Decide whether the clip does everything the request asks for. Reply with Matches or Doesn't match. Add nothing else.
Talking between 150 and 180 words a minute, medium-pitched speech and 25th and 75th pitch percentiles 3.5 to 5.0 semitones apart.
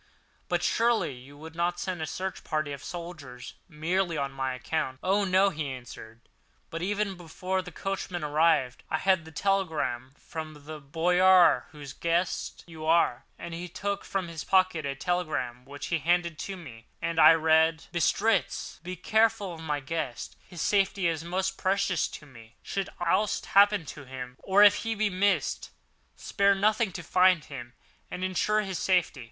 Matches